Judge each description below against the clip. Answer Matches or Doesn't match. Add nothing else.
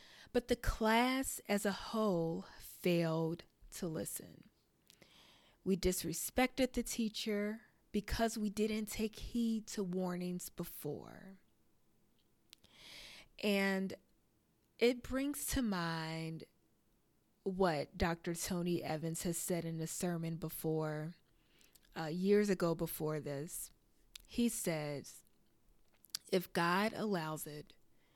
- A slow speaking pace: Matches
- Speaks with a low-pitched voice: Doesn't match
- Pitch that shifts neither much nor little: Matches